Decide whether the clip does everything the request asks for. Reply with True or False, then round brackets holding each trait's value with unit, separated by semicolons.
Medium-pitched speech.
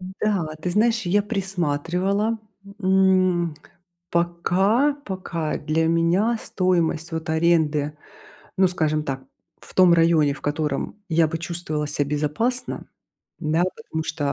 True (170 Hz)